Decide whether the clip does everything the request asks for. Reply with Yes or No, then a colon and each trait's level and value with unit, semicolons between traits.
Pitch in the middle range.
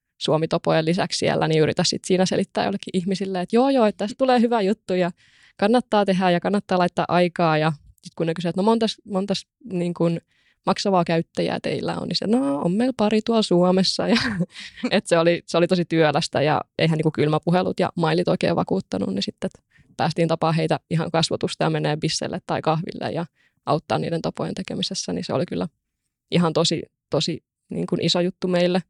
Yes: medium, 180 Hz